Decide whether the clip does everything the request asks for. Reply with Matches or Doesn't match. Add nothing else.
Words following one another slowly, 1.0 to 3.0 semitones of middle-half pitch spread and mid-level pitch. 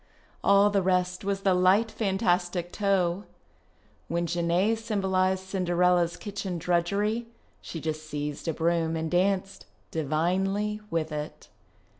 Matches